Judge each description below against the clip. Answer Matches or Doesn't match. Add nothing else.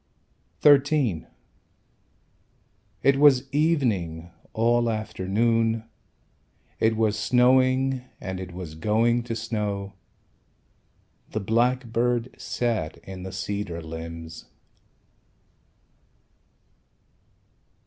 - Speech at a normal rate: Doesn't match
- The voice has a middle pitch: Doesn't match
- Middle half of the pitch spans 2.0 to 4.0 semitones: Doesn't match